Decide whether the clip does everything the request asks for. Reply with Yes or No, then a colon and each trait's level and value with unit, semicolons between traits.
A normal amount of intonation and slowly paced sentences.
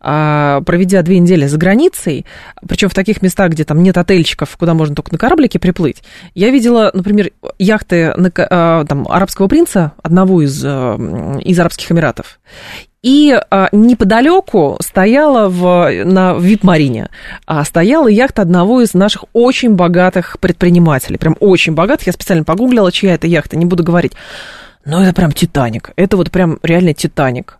No: average, 3.5 semitones; average, 150 wpm